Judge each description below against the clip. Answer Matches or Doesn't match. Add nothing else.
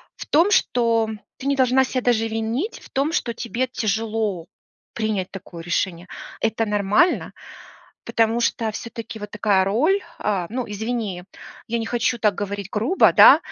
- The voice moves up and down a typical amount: Matches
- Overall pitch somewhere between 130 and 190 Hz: Doesn't match